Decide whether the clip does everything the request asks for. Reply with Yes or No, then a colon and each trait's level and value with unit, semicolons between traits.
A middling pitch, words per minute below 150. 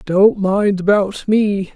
No: high, 200 Hz; slow, 135 wpm